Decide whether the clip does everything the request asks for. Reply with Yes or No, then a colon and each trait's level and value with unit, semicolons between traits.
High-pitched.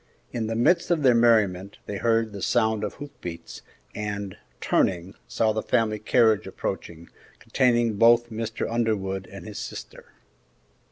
No: low, 110 Hz